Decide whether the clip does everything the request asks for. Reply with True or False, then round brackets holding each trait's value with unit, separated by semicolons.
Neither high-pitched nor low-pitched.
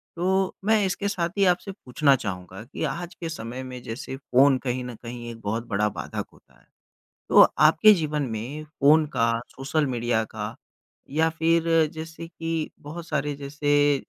True (145 Hz)